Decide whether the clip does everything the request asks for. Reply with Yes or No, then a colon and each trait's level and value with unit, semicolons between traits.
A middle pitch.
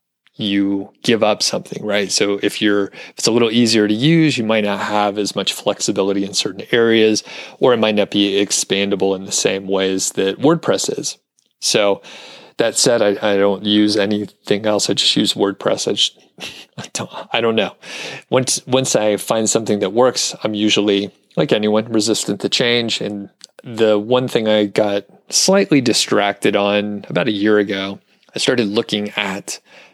No: low, 105 Hz